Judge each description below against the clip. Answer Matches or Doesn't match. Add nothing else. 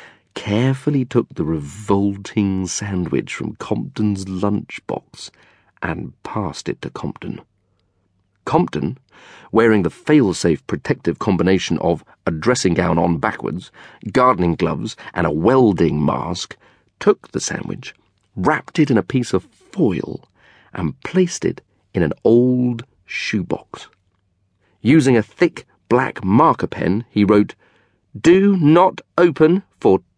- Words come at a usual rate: Doesn't match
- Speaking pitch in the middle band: Doesn't match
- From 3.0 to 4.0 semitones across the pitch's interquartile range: Doesn't match